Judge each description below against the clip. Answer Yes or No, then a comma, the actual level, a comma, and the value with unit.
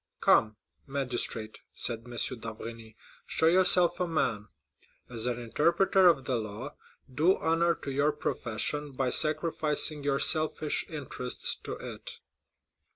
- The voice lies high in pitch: No, medium, 140 Hz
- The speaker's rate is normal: No, slow, 125 wpm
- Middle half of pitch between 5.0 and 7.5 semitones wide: Yes, average, 5.3 semitones